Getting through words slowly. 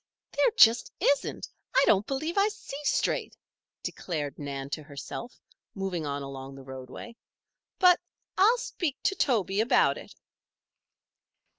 Yes: slow, 130 wpm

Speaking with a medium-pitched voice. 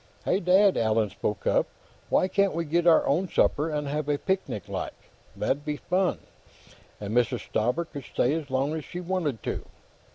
Yes: medium, 150 Hz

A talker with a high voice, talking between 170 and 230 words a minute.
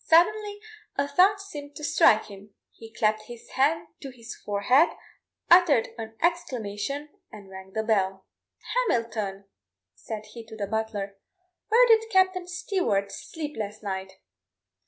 No: high, 230 Hz; slow, 135 wpm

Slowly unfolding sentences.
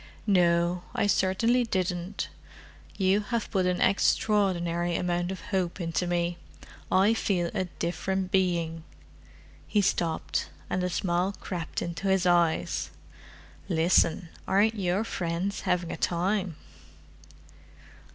Yes: slow, 110 wpm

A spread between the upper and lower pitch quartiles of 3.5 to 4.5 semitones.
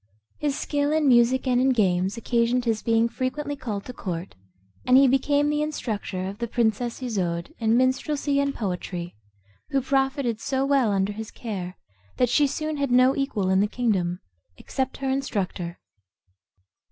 No: average, 4.9 semitones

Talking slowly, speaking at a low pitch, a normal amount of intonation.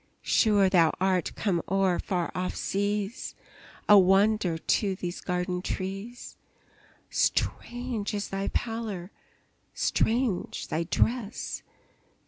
No: slow, 105 wpm; high, 195 Hz; average, 3.0 semitones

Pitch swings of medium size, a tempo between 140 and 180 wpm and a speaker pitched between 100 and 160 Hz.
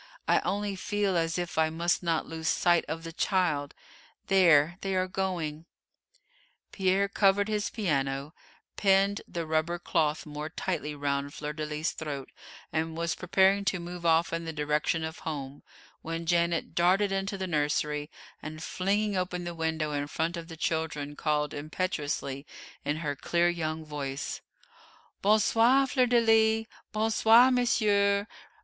No: average, 4.1 semitones; average, 155 wpm; medium, 170 Hz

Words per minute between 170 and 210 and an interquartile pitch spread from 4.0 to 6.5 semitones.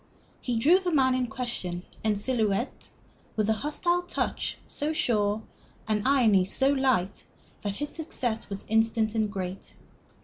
No: average, 145 wpm; average, 4.5 semitones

